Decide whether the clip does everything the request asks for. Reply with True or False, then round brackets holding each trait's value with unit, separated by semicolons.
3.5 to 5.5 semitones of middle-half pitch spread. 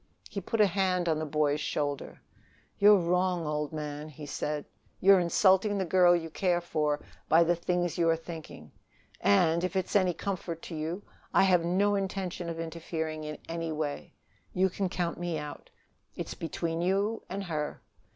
False (3.0 semitones)